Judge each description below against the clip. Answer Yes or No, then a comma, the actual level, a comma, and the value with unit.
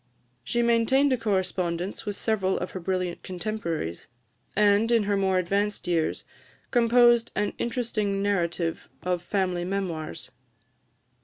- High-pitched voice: Yes, high, 195 Hz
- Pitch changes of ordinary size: Yes, average, 3.8 semitones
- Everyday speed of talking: No, slow, 125 wpm